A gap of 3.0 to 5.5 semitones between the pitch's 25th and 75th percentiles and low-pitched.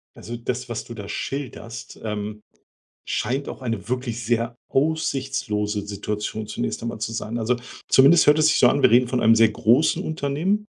Yes: average, 3.7 semitones; low, 120 Hz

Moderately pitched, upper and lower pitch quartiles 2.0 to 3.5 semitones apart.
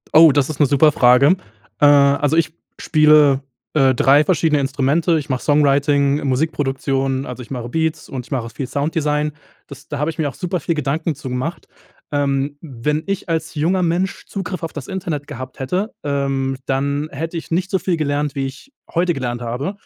Yes: medium, 145 Hz; average, 3.0 semitones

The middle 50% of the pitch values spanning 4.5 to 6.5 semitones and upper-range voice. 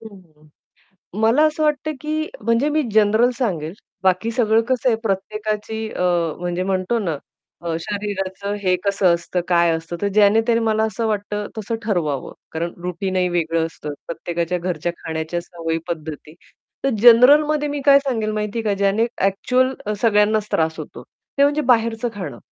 Yes: average, 4.8 semitones; high, 205 Hz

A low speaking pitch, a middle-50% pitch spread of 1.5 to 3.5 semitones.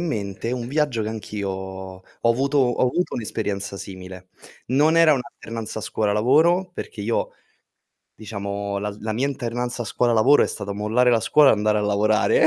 No: low, 110 Hz; average, 3.9 semitones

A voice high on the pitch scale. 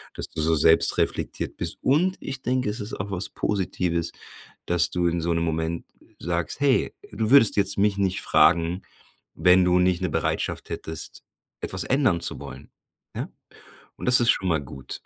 No: very low, 90 Hz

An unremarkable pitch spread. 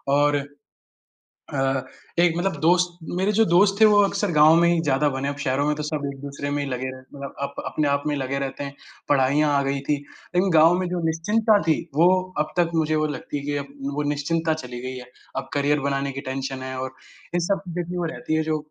Yes: average, 3.4 semitones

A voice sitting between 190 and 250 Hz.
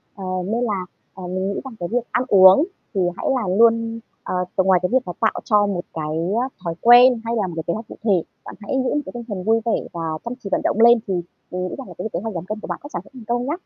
Yes: high, 215 Hz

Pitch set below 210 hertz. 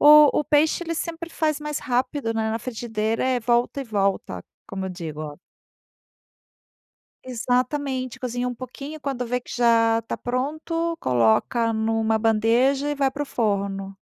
No: high, 245 Hz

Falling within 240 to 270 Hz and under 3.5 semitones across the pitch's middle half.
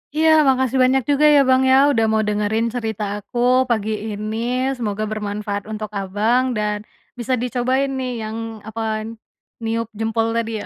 No: high, 225 Hz; average, 2.9 semitones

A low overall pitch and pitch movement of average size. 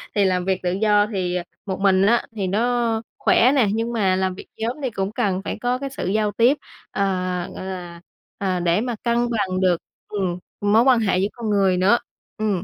No: high, 200 Hz; average, 3.5 semitones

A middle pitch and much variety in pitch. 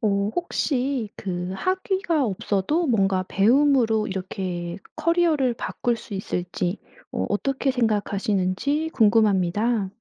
No: high, 215 Hz; wide, 6.0 semitones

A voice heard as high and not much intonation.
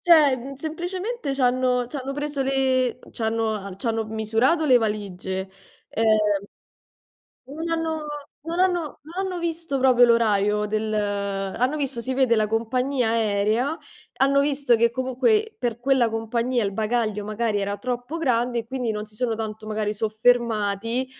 No: high, 240 Hz; average, 4.1 semitones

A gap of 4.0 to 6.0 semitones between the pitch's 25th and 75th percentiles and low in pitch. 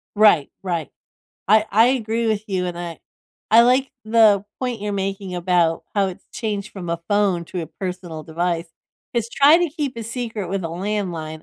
No: average, 4.3 semitones; high, 200 Hz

